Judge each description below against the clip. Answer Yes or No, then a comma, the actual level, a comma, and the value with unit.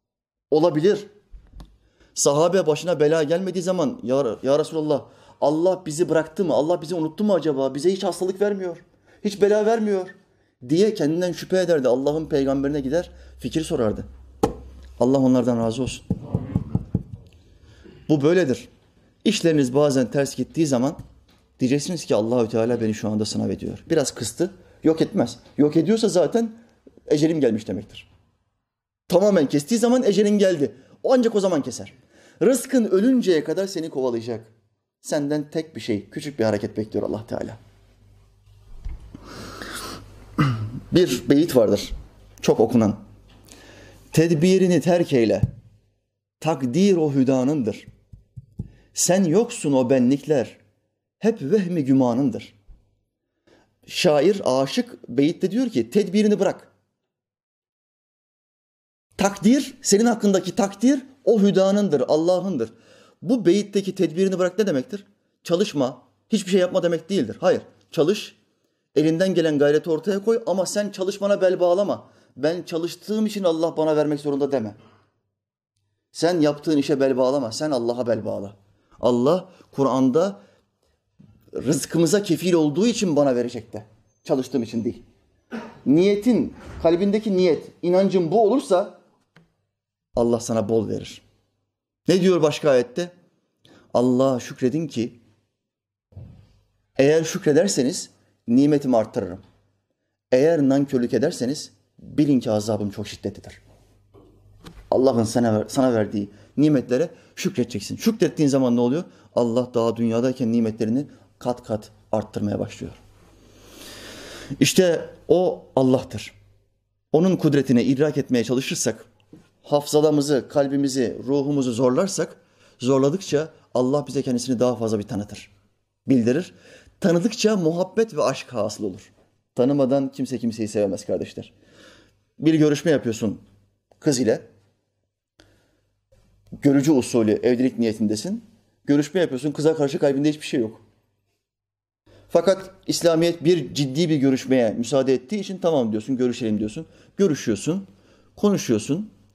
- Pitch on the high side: No, low, 135 Hz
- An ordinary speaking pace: Yes, average, 115 wpm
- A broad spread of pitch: Yes, wide, 8.2 semitones